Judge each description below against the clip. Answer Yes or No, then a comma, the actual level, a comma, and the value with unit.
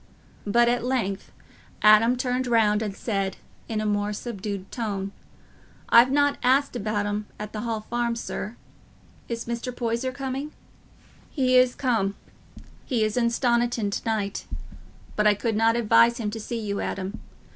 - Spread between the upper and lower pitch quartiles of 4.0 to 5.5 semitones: No, average, 2.7 semitones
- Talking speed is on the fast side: No, average, 155 wpm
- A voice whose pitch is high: Yes, high, 230 Hz